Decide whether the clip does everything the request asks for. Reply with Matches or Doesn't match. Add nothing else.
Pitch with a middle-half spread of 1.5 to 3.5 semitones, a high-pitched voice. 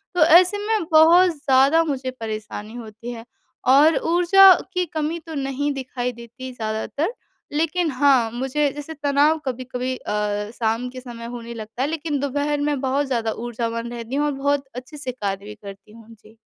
Doesn't match